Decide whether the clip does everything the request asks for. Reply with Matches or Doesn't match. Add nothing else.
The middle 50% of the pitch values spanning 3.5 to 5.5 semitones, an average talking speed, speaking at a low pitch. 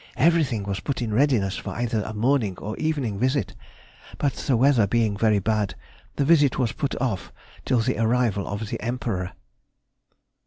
Matches